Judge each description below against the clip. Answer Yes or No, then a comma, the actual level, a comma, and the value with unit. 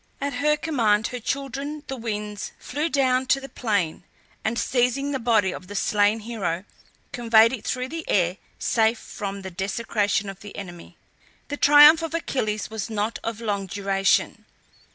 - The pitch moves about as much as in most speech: Yes, average, 4.7 semitones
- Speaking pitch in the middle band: No, high, 225 Hz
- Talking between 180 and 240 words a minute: No, average, 165 wpm